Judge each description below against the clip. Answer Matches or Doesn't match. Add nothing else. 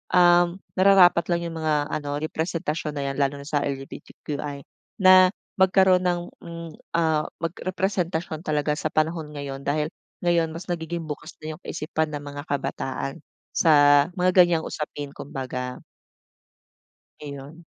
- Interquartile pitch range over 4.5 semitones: Doesn't match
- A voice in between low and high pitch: Matches